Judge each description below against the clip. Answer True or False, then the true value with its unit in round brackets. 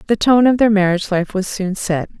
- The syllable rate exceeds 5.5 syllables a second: True (5.7 syllables/s)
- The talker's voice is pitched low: False (200 Hz)